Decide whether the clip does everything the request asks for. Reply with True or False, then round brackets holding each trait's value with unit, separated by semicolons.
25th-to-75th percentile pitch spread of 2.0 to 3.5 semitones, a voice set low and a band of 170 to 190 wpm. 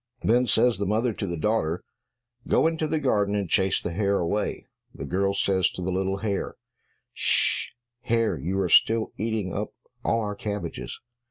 True (3.0 semitones; 100 Hz; 180 wpm)